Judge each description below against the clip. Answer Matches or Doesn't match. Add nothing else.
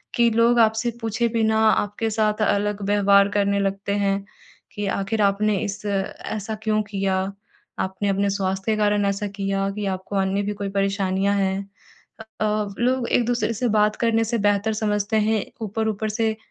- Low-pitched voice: Doesn't match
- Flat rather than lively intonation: Matches